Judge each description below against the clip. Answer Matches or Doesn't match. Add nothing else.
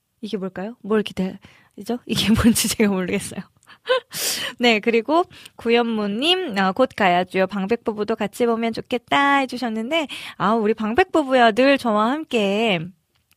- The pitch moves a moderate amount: Matches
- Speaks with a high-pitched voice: Matches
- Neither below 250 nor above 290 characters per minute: Matches